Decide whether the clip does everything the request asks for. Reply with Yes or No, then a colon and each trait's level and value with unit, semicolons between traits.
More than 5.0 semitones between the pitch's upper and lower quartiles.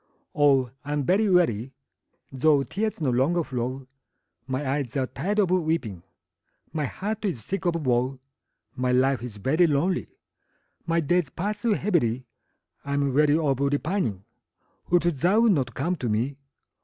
Yes: wide, 5.4 semitones